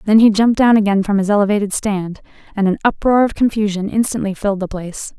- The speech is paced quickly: Yes, fast, 210 wpm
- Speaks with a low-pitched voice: No, high, 205 Hz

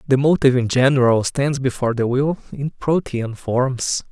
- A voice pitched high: No, low, 130 Hz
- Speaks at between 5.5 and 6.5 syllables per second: No, 4.9 syllables/s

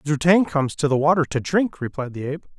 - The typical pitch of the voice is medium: Yes, medium, 150 Hz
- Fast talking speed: Yes, fast, 255 wpm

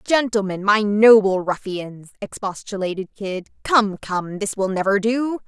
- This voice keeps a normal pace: No, slow, 120 wpm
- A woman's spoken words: Yes, female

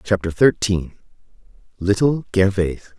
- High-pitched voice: No, low, 100 Hz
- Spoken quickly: No, slow, 60 wpm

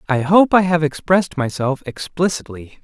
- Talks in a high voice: No, medium, 160 Hz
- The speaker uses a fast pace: No, average, 150 wpm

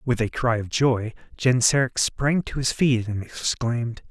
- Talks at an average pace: Yes, average, 175 wpm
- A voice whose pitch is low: Yes, low, 125 Hz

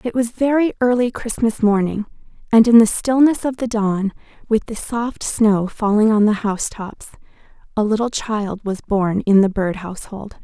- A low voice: No, high, 220 Hz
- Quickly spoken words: No, average, 170 wpm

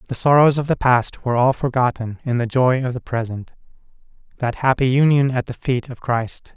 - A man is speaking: Yes, male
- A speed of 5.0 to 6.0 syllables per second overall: Yes, 5.3 syllables/s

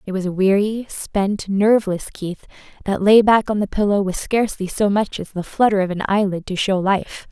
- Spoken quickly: Yes, fast, 215 wpm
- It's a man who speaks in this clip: No, female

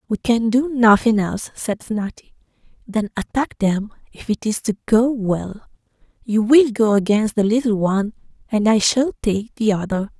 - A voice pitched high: Yes, high, 220 Hz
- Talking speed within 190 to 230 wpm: No, average, 170 wpm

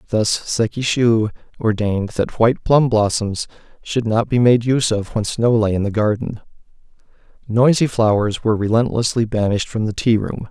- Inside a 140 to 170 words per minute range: Yes, average, 160 wpm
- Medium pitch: No, low, 110 Hz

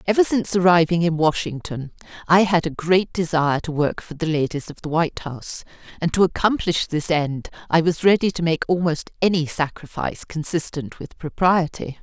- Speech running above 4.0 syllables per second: Yes, 5.4 syllables/s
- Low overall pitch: No, medium, 165 Hz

